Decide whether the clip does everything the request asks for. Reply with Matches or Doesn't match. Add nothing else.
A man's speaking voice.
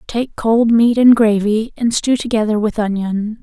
Doesn't match